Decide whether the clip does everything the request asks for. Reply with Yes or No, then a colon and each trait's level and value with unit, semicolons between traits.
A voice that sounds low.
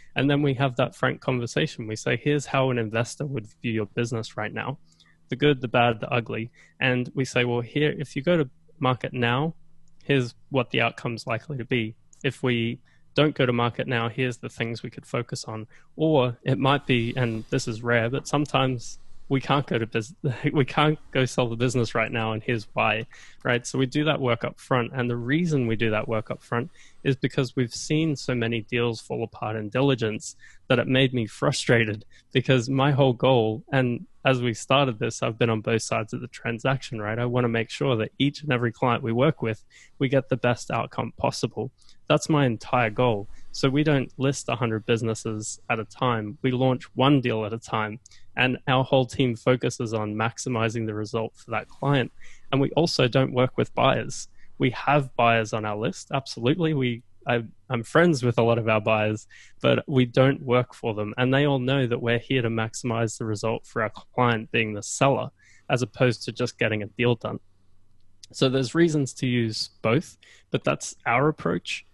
Yes: low, 125 Hz